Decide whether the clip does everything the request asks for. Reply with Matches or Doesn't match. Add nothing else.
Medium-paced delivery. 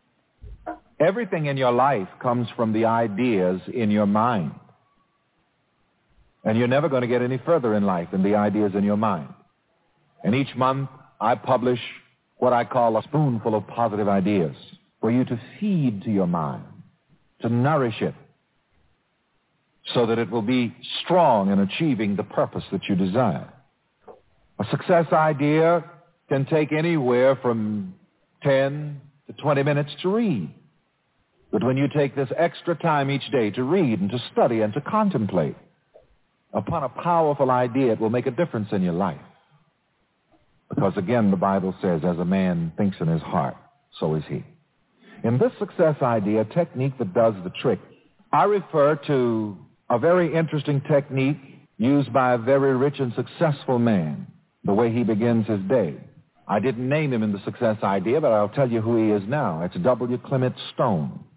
Matches